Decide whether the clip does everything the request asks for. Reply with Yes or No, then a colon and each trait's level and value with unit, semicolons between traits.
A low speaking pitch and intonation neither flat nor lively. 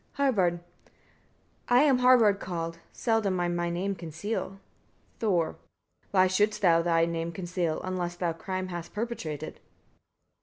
No: medium, 185 Hz; average, 3.5 semitones